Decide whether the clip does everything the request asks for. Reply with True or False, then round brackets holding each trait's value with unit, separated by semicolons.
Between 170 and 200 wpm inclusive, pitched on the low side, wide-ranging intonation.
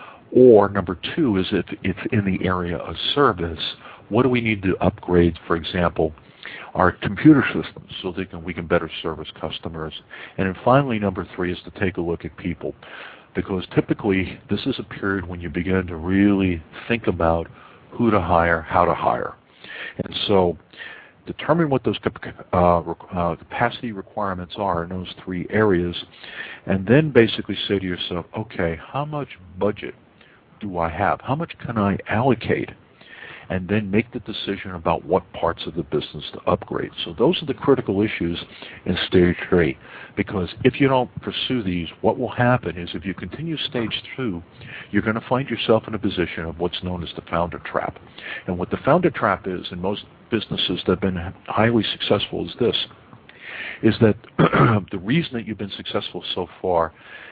False (175 wpm; 95 Hz; 4.5 semitones)